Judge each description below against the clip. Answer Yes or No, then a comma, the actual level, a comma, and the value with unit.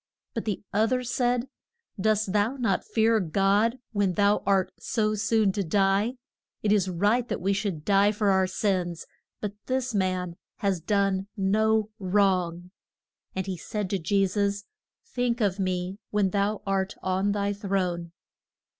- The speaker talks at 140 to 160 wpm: Yes, average, 155 wpm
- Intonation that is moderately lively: No, narrow, 2.2 semitones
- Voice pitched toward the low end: No, high, 200 Hz